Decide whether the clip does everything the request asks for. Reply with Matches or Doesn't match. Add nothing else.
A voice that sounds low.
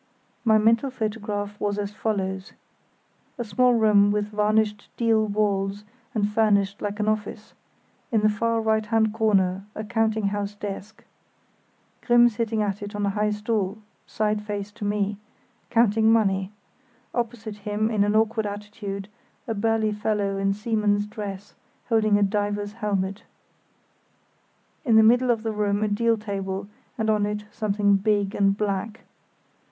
Doesn't match